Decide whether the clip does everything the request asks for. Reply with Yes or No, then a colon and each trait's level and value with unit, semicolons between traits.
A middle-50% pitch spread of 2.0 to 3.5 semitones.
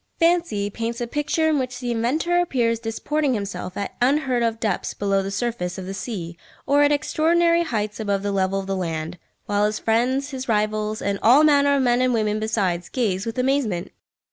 No: wide, 5.4 semitones